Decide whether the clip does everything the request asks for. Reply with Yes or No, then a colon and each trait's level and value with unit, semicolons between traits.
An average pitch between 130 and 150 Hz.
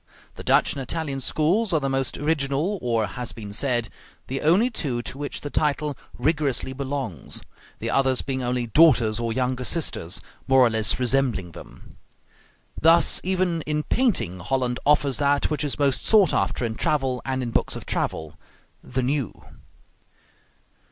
Yes: low, 135 Hz